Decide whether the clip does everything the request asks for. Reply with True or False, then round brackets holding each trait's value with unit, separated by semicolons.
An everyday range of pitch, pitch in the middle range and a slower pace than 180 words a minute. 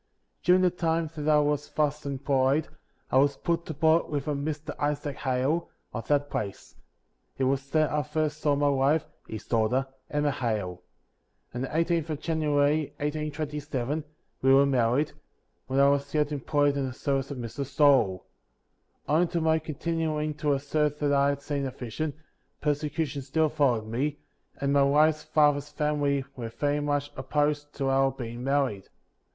False (2.0 semitones; 145 Hz; 170 wpm)